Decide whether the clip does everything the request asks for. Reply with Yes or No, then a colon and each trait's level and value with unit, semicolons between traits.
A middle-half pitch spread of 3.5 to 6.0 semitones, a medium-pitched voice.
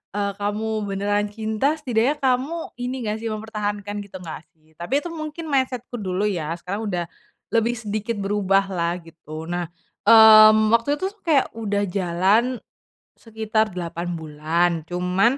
No: average, 3.8 semitones; high, 210 Hz